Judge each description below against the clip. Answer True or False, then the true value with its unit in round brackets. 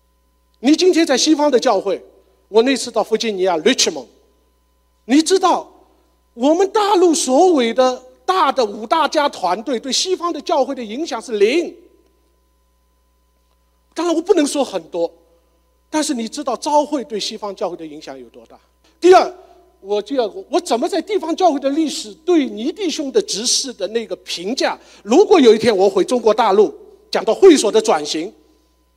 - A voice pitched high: True (260 Hz)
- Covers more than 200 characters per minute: True (260 characters per minute)